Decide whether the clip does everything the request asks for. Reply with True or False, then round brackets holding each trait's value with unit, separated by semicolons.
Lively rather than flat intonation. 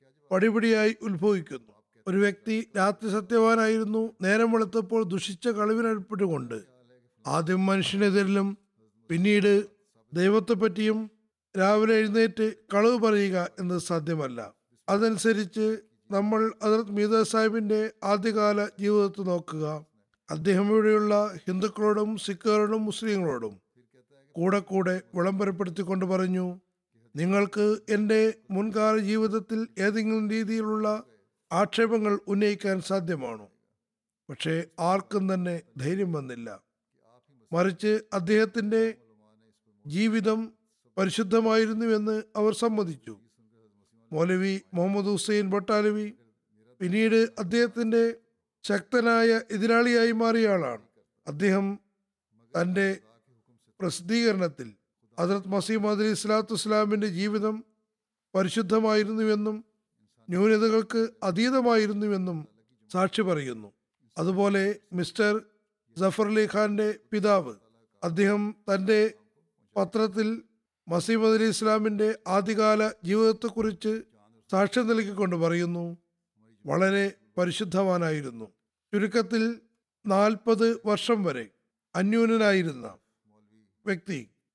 False (3.6 semitones)